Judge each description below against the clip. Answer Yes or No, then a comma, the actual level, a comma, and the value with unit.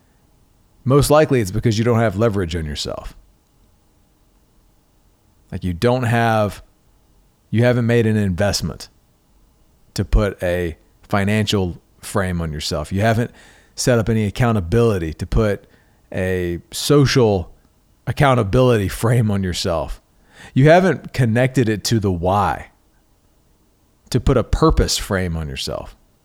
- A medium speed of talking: No, slow, 125 wpm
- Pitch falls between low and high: No, low, 105 Hz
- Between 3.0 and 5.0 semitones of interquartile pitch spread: Yes, average, 4.4 semitones